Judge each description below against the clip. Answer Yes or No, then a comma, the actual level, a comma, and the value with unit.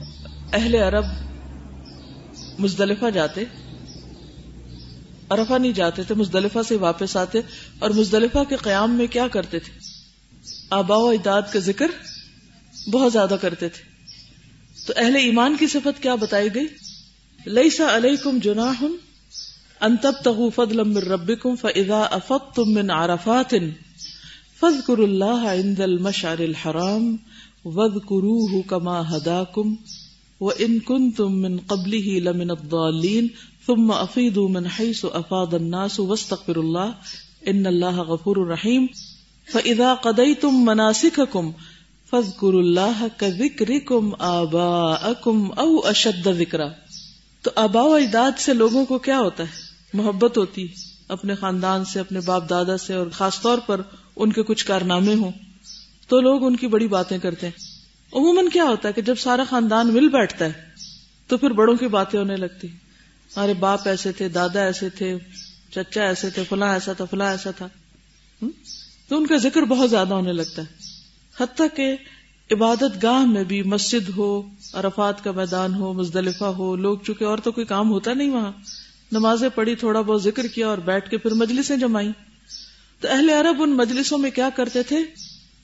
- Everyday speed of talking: Yes, average, 135 wpm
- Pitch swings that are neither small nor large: Yes, average, 4.3 semitones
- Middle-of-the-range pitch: No, high, 205 Hz